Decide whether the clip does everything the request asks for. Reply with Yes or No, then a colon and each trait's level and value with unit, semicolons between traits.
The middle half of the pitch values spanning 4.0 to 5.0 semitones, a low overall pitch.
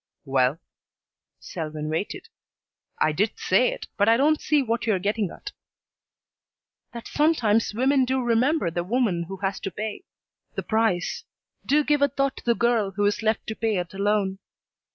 No: average, 4.7 semitones; high, 220 Hz